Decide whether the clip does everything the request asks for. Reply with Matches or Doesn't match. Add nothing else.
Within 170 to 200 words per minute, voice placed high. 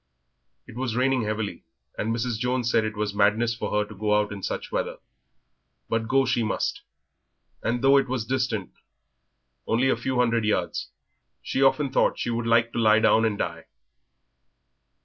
Doesn't match